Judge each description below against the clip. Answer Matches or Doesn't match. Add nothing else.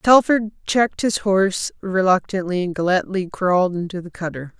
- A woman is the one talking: Matches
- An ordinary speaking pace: Matches